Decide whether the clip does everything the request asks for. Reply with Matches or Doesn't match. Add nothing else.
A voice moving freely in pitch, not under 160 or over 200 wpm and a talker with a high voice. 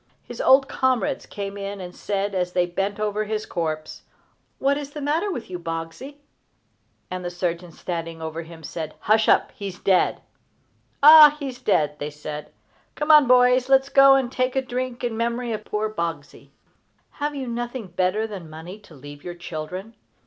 Matches